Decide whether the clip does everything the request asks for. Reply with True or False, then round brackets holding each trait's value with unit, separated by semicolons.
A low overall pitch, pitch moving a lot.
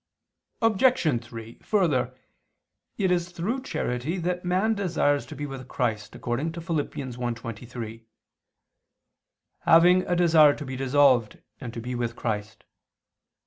False (145 Hz; 6.6 semitones)